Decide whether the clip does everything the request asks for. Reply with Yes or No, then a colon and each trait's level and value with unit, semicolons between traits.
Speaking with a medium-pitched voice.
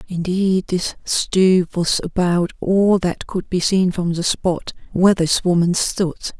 Yes: medium, 180 Hz